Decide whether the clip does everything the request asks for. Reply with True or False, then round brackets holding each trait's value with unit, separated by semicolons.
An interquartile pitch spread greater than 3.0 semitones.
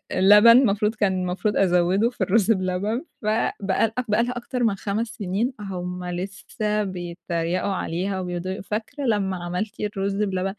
False (2.7 semitones)